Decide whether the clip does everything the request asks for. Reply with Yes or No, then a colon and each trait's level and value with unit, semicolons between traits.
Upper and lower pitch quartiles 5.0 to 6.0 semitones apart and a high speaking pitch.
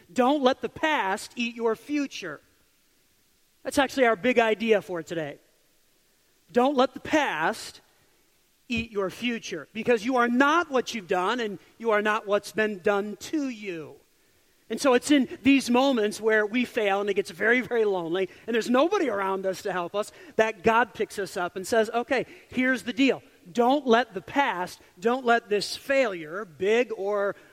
No: average, 3.9 semitones; high, 230 Hz